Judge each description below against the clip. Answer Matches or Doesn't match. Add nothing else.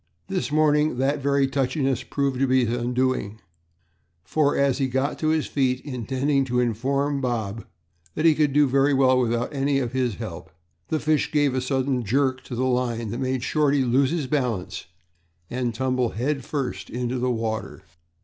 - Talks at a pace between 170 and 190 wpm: Matches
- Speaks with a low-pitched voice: Matches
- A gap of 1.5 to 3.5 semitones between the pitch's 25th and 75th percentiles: Matches